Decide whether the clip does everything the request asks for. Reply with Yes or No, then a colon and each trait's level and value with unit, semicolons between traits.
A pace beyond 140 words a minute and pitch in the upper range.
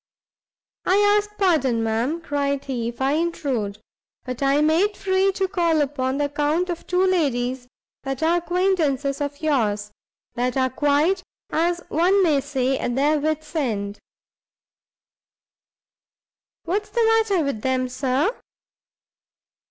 No: slow, 135 wpm; very high, 290 Hz